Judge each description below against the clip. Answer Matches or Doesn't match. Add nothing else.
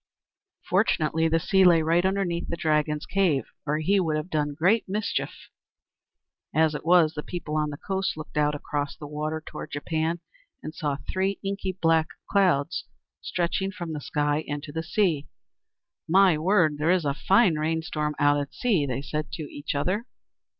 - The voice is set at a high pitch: Doesn't match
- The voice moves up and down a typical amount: Matches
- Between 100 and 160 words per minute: Doesn't match